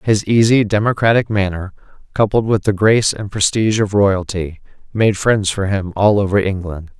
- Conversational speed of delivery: Yes, average, 165 wpm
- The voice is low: Yes, low, 100 Hz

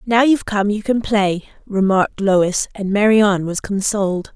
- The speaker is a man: No, female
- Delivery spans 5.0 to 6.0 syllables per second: No, 4.8 syllables/s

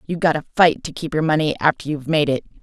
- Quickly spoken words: Yes, fast, 275 wpm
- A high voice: No, medium, 155 Hz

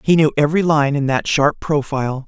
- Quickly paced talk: Yes, fast, 210 wpm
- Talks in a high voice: No, medium, 145 Hz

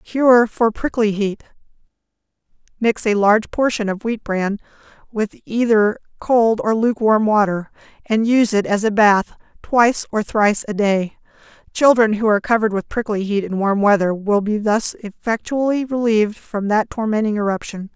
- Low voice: No, high, 215 Hz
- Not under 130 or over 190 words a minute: Yes, average, 155 wpm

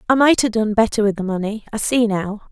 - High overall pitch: Yes, high, 215 Hz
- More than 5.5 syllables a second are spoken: Yes, 6.0 syllables/s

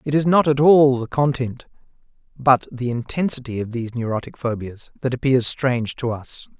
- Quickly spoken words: No, average, 175 wpm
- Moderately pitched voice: No, low, 130 Hz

